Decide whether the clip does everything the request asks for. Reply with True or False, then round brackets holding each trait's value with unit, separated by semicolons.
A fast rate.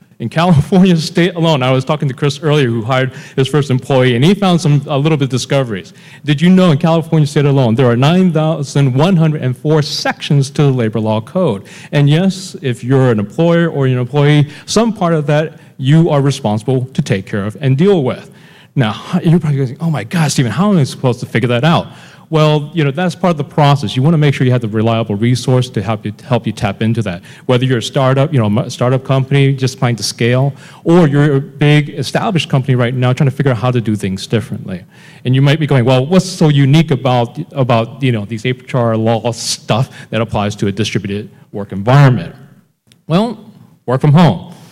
True (225 wpm)